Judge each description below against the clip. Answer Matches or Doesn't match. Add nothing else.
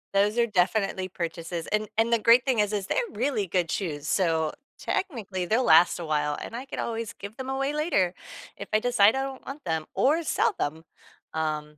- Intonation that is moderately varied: Doesn't match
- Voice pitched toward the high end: Matches